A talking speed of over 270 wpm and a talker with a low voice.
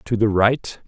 No: fast, 205 wpm; low, 110 Hz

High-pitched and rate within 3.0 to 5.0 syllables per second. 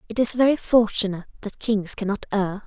No: high, 210 Hz; 5.9 syllables/s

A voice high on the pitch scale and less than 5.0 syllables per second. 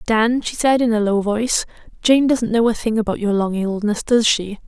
No: high, 220 Hz; 5.1 syllables/s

